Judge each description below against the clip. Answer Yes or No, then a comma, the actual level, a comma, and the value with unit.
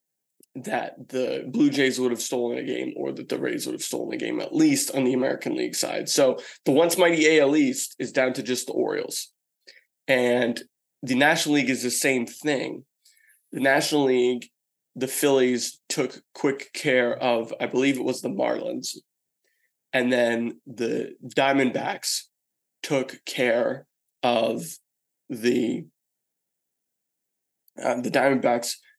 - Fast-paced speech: No, average, 145 wpm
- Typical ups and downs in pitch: Yes, average, 3.8 semitones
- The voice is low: Yes, low, 130 Hz